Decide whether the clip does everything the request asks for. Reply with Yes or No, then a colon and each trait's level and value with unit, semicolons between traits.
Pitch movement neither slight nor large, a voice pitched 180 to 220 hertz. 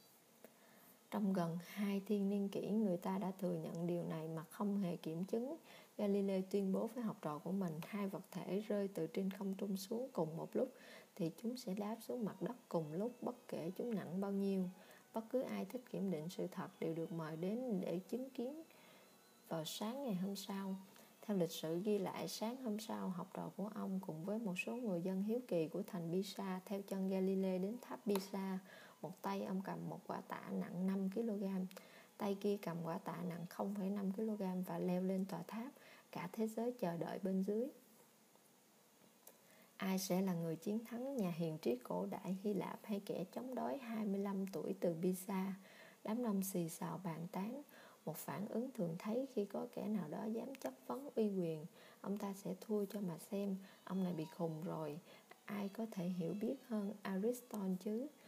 Yes: average, 3.6 semitones; high, 200 Hz